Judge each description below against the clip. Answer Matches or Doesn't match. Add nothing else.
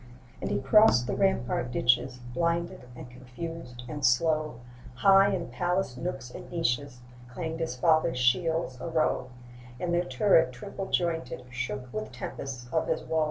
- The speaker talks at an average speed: Matches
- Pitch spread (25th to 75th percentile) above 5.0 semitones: Matches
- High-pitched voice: Doesn't match